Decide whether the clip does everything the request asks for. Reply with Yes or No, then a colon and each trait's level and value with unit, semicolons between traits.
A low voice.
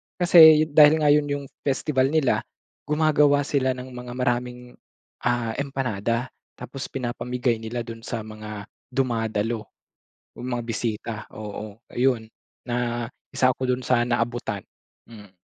Yes: low, 125 Hz